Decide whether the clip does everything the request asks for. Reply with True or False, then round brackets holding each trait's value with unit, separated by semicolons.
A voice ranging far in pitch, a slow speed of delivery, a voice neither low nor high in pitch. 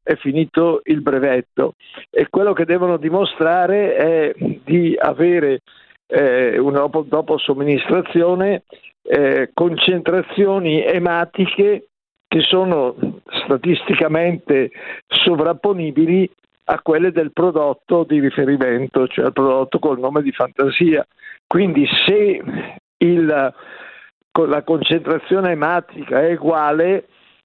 False (3.8 semitones; 105 wpm; 170 Hz)